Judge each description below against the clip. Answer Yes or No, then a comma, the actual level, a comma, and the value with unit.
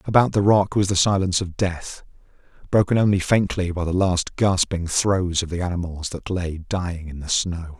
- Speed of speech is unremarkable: Yes, average, 190 wpm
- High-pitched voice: No, very low, 90 Hz